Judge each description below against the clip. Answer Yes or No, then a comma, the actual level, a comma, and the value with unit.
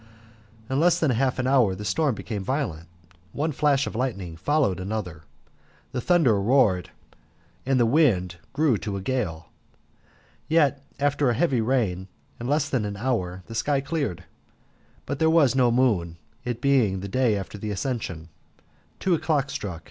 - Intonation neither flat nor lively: No, wide, 6.1 semitones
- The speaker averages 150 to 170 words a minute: Yes, average, 165 wpm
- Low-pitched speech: Yes, low, 125 Hz